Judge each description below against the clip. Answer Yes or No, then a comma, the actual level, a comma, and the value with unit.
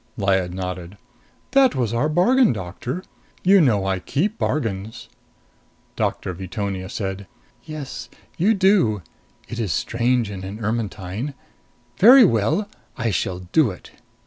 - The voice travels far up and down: Yes, wide, 8.2 semitones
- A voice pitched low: Yes, low, 115 Hz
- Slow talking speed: Yes, slow, 125 wpm